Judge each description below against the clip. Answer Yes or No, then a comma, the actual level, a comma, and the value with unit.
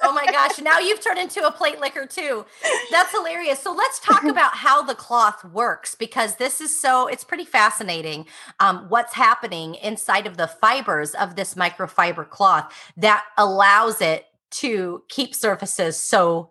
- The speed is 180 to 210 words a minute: No, average, 165 wpm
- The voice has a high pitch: Yes, high, 235 Hz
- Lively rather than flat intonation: Yes, wide, 7.3 semitones